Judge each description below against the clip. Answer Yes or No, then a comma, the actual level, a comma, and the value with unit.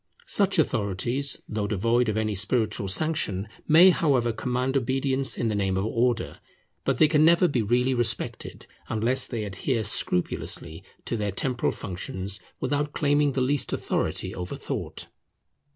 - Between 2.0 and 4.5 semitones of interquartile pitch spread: No, average, 5.2 semitones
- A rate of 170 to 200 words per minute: No, average, 150 wpm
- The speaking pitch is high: No, low, 120 Hz